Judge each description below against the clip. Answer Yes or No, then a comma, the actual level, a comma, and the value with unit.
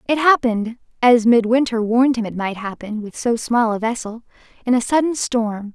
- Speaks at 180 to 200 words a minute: Yes, average, 190 wpm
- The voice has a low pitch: No, high, 235 Hz